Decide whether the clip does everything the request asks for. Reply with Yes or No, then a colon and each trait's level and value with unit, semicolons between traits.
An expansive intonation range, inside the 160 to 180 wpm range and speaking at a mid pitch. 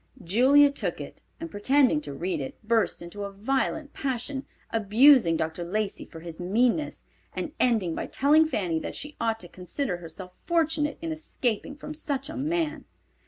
No: wide, 8.1 semitones; average, 165 wpm; high, 235 Hz